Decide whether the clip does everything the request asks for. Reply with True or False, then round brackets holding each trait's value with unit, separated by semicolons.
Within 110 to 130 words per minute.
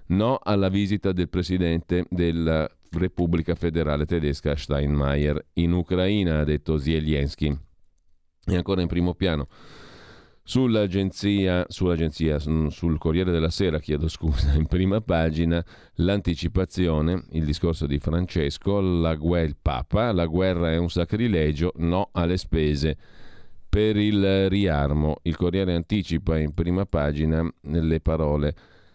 True (120 wpm)